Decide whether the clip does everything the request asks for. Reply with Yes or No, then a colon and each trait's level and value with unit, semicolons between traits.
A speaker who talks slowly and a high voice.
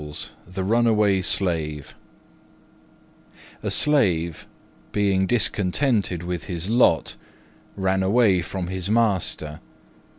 No: slow, 90 wpm; very low, 95 Hz